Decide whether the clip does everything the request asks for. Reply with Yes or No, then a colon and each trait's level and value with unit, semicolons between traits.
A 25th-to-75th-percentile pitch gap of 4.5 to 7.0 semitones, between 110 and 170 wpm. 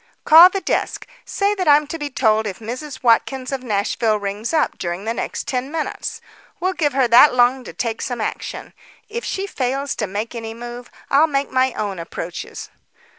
No: average, 4.8 semitones; average, 190 wpm